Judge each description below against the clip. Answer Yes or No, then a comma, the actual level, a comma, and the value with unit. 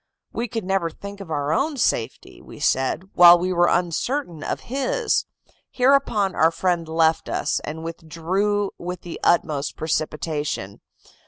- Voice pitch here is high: No, medium, 175 Hz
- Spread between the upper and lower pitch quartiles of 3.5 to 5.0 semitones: Yes, average, 4.1 semitones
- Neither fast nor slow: Yes, average, 145 wpm